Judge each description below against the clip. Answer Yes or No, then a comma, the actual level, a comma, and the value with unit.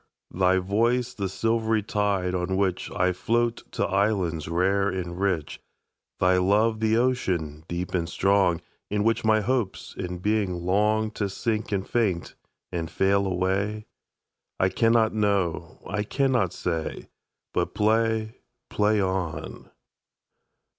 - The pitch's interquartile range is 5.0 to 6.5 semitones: No, average, 3.2 semitones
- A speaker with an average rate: No, slow, 115 wpm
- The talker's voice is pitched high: No, low, 100 Hz